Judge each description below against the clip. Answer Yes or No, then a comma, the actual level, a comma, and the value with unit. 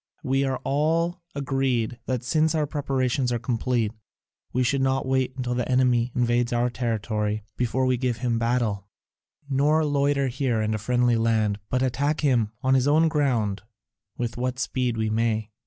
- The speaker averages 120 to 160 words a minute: No, average, 170 wpm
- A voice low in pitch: Yes, low, 125 Hz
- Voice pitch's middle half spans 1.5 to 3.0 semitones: Yes, narrow, 2.6 semitones